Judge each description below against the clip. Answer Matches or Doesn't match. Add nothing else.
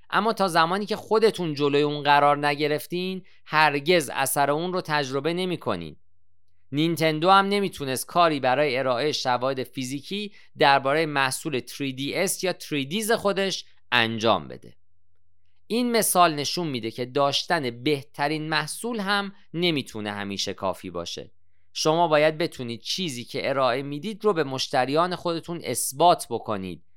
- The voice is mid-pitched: Matches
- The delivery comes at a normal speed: Matches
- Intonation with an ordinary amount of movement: Doesn't match